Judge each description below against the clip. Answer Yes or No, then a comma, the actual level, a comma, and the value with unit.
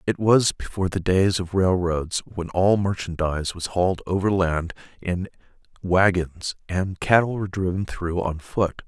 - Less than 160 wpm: Yes, average, 150 wpm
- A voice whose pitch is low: Yes, very low, 90 Hz